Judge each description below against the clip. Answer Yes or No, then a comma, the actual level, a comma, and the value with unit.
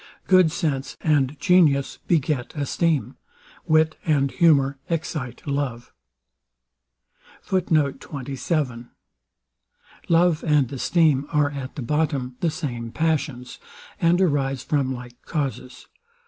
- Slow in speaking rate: Yes, slow, 95 wpm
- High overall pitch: No, medium, 145 Hz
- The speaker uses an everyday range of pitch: Yes, average, 3.4 semitones